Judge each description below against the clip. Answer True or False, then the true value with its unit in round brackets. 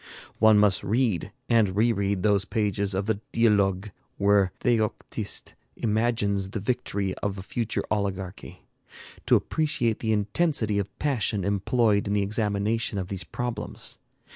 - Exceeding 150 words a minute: False (140 wpm)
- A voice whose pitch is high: False (105 Hz)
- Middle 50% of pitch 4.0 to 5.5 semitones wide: False (2.4 semitones)